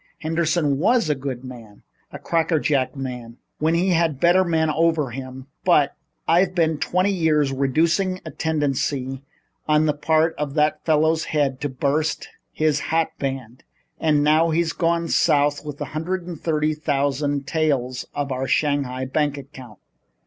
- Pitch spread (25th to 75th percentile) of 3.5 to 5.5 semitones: No, average, 3.1 semitones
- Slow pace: No, average, 155 wpm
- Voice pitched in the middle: Yes, medium, 150 Hz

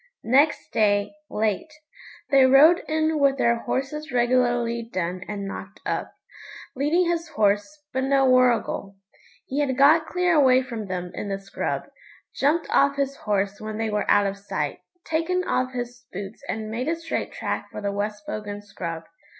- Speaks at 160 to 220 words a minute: Yes, average, 165 wpm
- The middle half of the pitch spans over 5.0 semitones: Yes, wide, 5.5 semitones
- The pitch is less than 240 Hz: No, high, 245 Hz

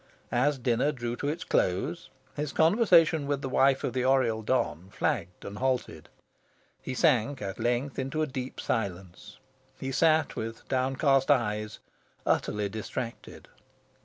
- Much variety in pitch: No, average, 4.2 semitones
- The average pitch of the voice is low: Yes, low, 130 Hz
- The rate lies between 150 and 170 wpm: No, average, 140 wpm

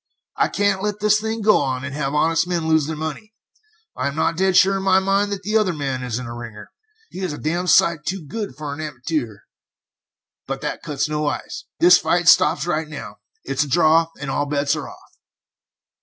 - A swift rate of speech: Yes, fast, 215 wpm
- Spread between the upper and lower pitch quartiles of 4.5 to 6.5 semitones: Yes, average, 4.9 semitones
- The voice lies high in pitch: No, medium, 160 Hz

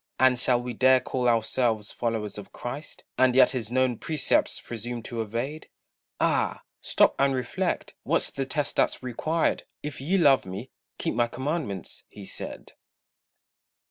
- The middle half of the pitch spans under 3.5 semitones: Yes, narrow, 2.6 semitones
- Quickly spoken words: No, average, 150 wpm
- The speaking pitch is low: Yes, low, 125 Hz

